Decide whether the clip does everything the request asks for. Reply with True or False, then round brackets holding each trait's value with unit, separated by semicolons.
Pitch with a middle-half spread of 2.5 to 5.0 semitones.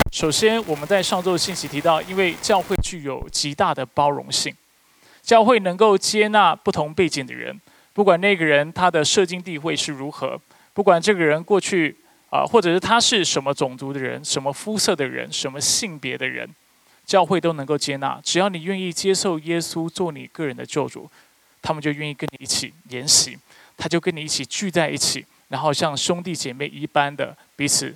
True (4.7 semitones)